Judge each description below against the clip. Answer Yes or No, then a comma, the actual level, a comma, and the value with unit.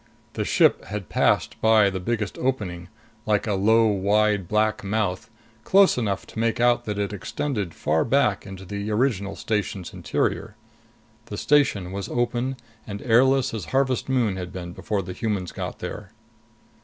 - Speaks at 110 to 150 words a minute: No, average, 160 wpm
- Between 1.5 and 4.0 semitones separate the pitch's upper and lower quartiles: Yes, average, 3.6 semitones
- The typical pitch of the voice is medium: No, low, 105 Hz